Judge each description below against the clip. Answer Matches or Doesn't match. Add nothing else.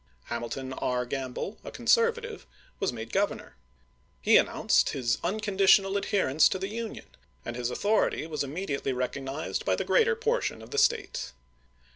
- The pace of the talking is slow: Doesn't match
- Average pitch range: Doesn't match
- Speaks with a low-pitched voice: Doesn't match